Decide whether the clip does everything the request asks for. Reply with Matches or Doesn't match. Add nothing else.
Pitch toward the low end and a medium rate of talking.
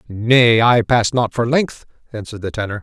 Matches